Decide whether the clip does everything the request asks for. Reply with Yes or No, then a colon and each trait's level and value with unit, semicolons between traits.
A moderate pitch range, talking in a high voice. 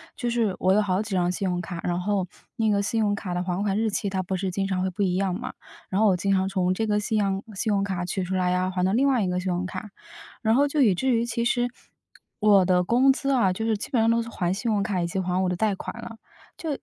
Yes: average, 3.3 semitones; high, 195 Hz